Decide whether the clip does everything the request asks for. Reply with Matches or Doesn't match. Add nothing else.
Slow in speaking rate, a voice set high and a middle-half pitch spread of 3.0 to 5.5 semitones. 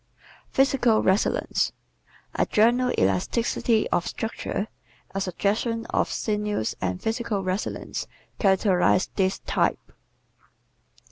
Matches